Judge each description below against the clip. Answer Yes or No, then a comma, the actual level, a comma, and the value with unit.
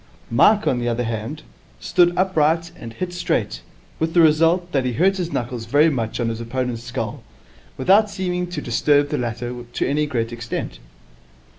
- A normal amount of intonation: No, wide, 6.7 semitones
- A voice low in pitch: No, medium, 145 Hz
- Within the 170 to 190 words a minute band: Yes, average, 175 wpm